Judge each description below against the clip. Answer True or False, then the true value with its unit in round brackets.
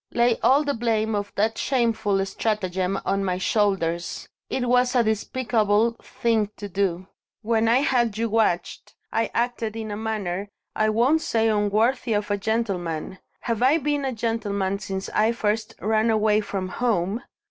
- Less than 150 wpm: False (160 wpm)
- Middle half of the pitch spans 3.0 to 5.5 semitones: False (2.6 semitones)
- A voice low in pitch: False (220 Hz)